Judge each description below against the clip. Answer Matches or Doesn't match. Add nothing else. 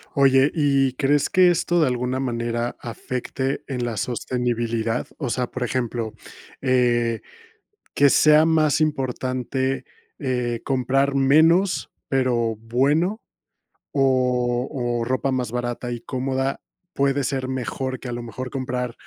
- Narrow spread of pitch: Matches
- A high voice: Doesn't match